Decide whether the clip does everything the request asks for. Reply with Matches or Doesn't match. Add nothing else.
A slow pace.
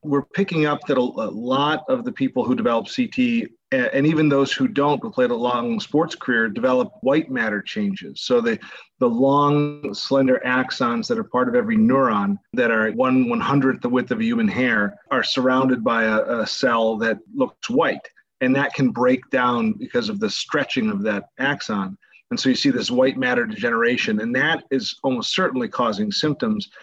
Doesn't match